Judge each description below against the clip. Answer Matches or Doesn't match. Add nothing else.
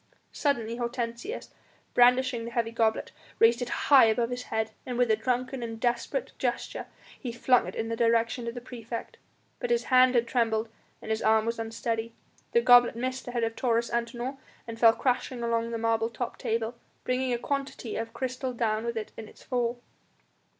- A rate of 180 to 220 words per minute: Matches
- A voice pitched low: Doesn't match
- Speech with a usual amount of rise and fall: Doesn't match